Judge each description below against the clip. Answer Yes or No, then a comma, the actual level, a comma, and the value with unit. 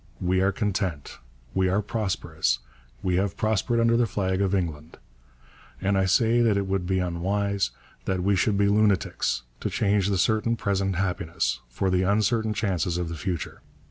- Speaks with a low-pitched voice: Yes, very low, 95 Hz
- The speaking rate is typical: Yes, average, 175 wpm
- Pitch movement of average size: No, narrow, 2.2 semitones